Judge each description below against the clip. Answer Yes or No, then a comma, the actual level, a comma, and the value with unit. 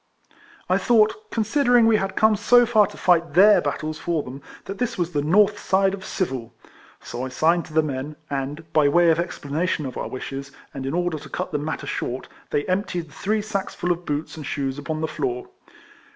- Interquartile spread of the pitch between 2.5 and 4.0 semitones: No, average, 5.3 semitones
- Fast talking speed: Yes, fast, 210 wpm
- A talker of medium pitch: Yes, medium, 165 Hz